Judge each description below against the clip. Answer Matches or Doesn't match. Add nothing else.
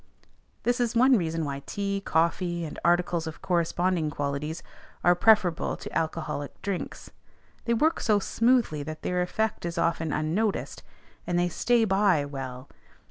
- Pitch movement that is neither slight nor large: Matches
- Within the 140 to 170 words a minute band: Matches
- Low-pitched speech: Doesn't match